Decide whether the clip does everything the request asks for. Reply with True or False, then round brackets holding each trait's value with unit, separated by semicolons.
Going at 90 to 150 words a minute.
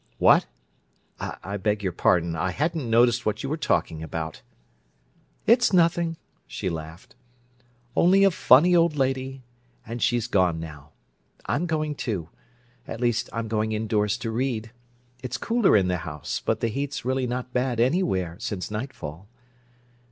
True (145 wpm)